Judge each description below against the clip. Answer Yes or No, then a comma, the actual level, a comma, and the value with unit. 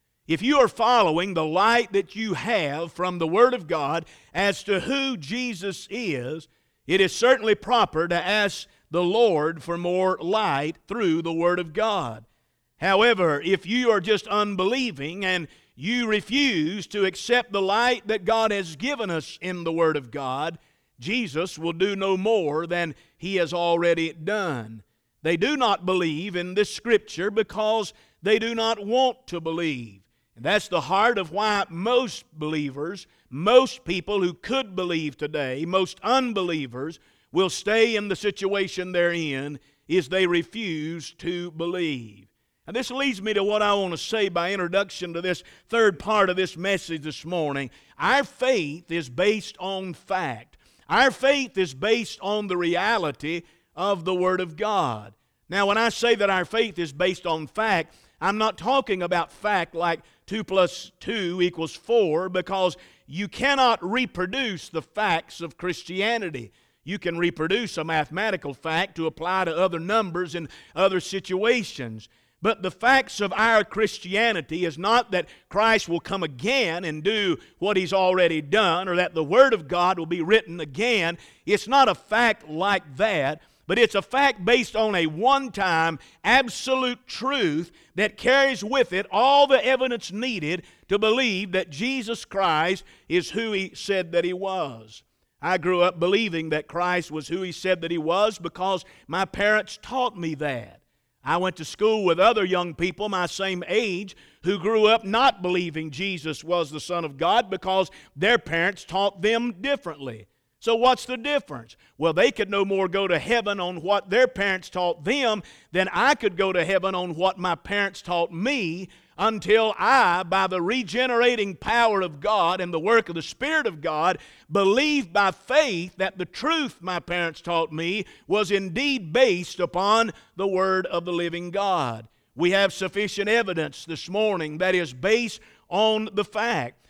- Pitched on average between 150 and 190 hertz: Yes, medium, 185 Hz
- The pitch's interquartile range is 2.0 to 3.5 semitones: No, average, 4.4 semitones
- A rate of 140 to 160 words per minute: No, average, 170 wpm